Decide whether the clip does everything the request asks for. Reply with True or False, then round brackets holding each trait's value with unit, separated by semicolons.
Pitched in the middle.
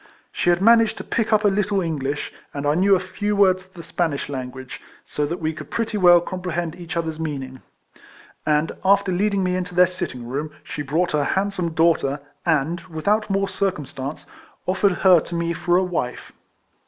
True (175 Hz)